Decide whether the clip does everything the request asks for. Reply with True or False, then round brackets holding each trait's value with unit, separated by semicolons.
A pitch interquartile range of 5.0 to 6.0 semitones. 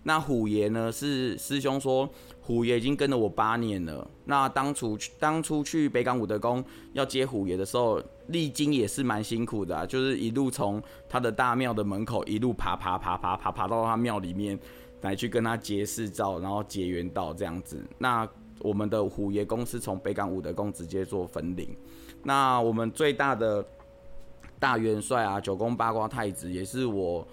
False (4.4 semitones)